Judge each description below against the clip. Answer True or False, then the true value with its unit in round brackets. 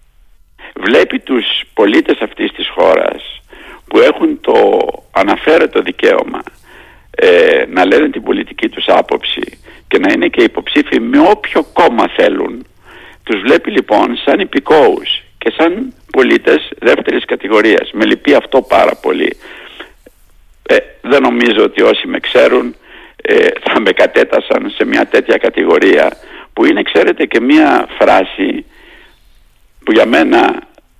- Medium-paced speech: True (130 wpm)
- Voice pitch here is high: True (375 Hz)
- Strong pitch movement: True (5.9 semitones)